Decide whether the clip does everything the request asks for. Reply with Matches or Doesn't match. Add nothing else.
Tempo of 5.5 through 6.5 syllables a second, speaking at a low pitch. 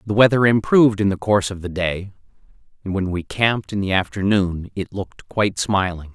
Matches